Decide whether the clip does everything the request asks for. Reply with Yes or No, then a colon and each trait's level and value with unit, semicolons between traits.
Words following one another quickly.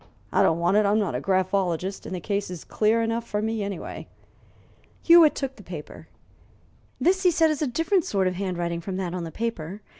Yes: fast, 210 wpm